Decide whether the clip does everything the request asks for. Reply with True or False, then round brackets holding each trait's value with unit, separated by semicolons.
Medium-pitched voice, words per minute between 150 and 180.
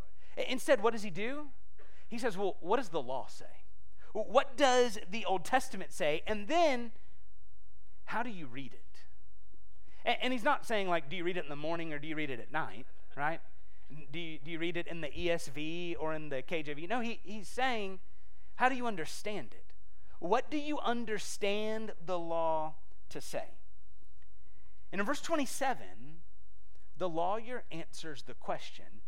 True (170 Hz; 175 wpm)